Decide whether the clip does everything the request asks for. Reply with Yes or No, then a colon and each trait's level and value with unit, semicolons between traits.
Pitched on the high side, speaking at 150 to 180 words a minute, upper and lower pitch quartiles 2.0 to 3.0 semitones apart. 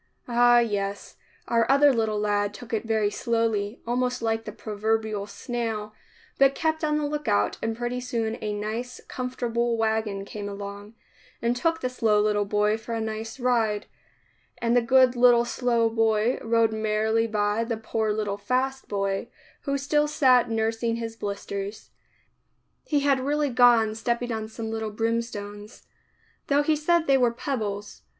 Yes: high, 225 Hz; average, 160 wpm; average, 2.7 semitones